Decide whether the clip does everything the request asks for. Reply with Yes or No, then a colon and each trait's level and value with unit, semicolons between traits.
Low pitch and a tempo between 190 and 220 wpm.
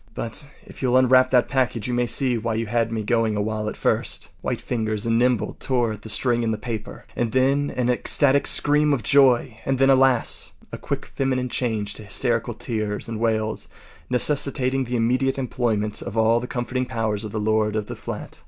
Yes: low, 120 Hz; average, 200 wpm